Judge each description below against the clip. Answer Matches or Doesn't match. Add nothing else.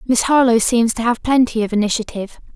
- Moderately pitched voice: Doesn't match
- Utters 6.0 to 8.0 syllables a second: Matches